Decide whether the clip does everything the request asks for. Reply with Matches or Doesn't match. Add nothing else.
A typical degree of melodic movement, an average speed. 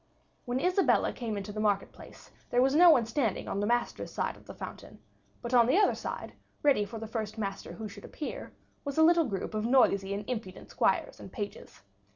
Doesn't match